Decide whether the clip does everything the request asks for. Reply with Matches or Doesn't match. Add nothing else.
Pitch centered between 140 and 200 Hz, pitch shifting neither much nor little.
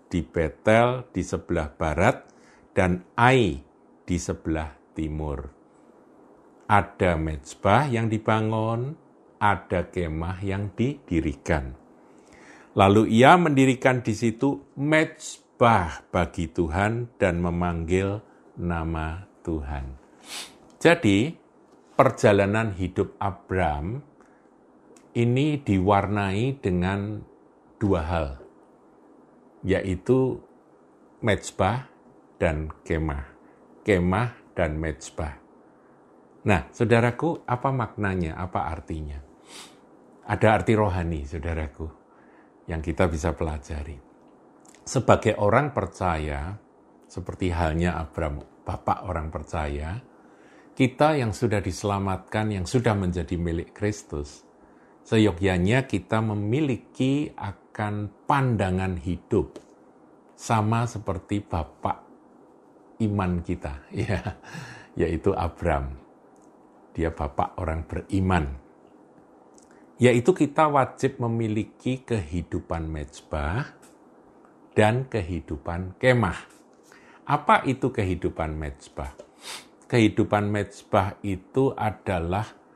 Doesn't match